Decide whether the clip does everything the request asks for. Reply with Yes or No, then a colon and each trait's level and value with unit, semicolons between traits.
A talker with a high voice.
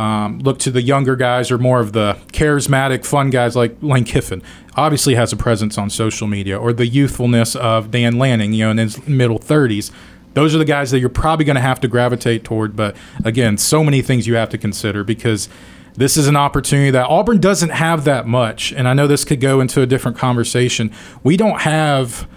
No: low, 125 Hz